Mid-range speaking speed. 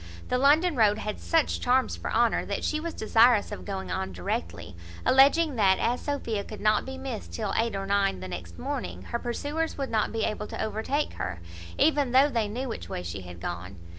No: fast, 210 wpm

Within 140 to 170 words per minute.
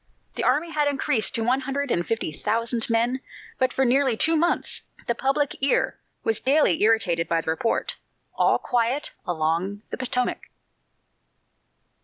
Yes: average, 150 wpm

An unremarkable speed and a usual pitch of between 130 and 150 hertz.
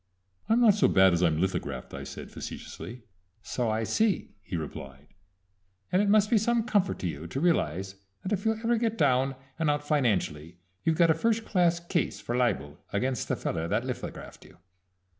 Yes: average, 190 wpm; medium, 140 Hz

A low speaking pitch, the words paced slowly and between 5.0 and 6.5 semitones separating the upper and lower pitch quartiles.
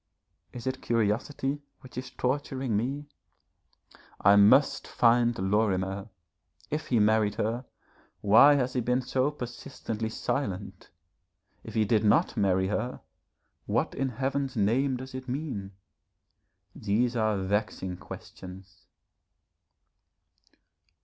No: low, 115 Hz; slow, 110 wpm; average, 4.2 semitones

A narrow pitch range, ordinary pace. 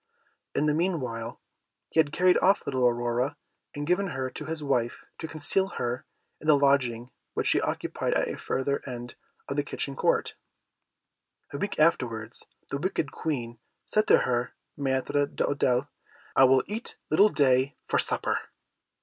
No: average, 3.8 semitones; average, 160 wpm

